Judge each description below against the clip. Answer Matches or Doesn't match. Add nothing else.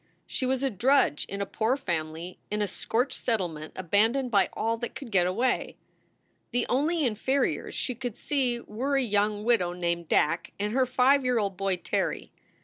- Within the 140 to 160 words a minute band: Doesn't match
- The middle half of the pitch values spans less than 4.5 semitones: Doesn't match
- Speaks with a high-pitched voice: Matches